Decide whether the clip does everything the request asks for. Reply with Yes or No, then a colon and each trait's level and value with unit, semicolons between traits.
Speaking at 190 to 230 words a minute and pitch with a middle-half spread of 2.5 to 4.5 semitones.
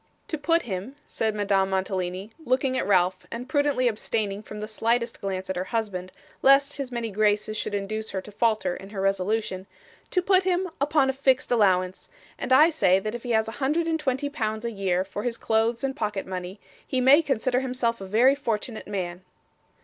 No: average, 200 wpm; average, 5.1 semitones